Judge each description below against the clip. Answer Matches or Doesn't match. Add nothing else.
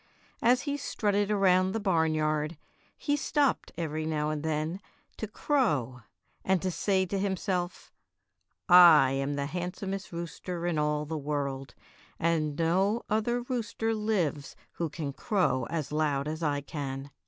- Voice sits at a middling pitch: Matches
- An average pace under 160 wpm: Matches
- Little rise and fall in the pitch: Doesn't match